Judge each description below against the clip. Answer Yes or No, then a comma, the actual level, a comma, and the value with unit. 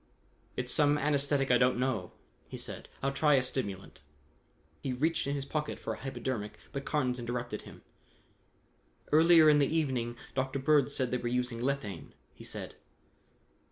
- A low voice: Yes, low, 130 Hz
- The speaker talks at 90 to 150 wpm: No, average, 160 wpm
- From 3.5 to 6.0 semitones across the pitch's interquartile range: No, average, 2.8 semitones